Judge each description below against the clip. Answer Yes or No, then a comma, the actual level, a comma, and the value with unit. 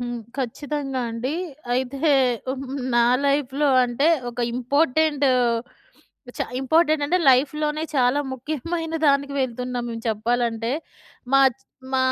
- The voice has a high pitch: Yes, very high, 270 Hz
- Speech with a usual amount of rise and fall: Yes, average, 3.2 semitones